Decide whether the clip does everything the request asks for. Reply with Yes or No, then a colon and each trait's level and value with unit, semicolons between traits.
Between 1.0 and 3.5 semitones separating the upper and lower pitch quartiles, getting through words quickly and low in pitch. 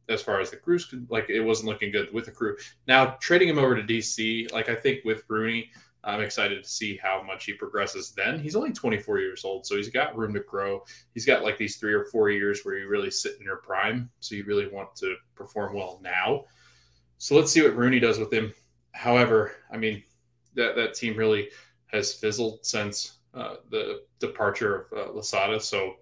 No: average, 4.5 semitones; fast, 210 wpm; low, 115 Hz